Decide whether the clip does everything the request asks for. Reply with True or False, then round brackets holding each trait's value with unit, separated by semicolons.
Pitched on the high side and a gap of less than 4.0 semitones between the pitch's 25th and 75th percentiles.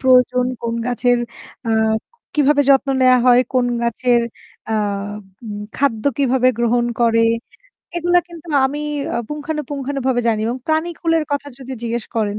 True (255 Hz; 3.3 semitones)